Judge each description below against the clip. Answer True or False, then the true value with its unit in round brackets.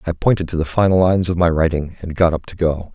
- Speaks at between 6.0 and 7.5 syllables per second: True (6.5 syllables/s)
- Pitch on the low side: True (85 Hz)